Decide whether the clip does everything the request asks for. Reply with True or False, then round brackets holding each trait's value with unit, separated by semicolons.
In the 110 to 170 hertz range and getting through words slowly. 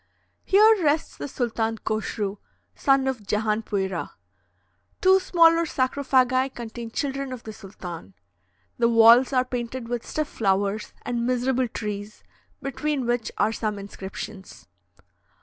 False (235 Hz; 120 wpm)